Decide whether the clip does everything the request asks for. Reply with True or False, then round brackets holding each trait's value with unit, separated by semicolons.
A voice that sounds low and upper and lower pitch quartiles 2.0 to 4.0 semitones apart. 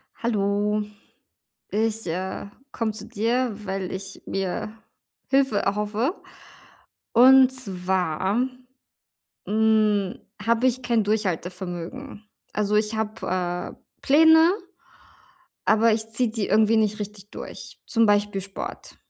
False (215 Hz; 2.8 semitones)